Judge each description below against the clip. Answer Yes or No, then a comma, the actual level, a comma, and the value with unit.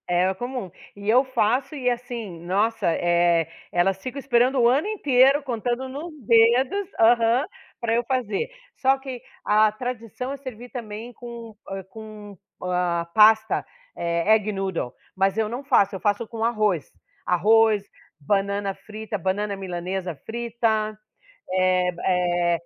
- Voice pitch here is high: Yes, high, 220 Hz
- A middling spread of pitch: Yes, average, 4.2 semitones